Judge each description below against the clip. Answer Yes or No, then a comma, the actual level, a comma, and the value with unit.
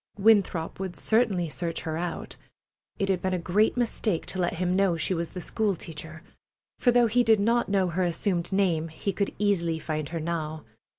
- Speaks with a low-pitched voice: No, medium, 180 Hz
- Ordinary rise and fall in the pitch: Yes, average, 3.4 semitones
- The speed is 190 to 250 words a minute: Yes, average, 195 wpm